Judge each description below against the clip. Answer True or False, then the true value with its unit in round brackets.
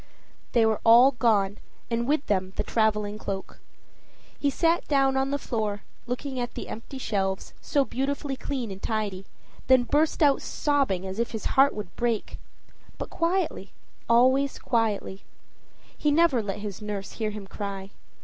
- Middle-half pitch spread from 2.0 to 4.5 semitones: False (4.9 semitones)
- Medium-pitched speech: False (230 Hz)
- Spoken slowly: False (160 wpm)